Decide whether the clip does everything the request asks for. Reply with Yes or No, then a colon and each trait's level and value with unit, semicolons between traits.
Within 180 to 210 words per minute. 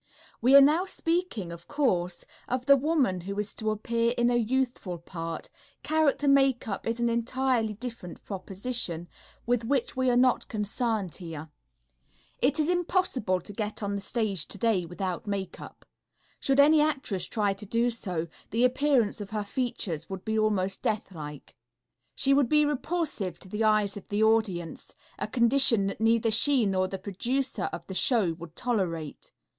No: average, 165 wpm